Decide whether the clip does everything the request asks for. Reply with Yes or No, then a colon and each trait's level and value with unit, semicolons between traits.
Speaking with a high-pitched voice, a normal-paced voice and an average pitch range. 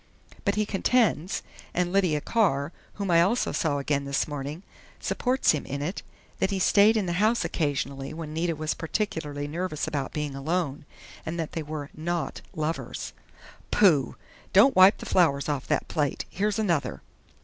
No: medium, 165 Hz; average, 165 wpm; average, 4.7 semitones